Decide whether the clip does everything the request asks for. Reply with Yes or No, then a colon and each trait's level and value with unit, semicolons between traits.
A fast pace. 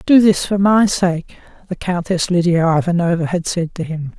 No: average, 185 wpm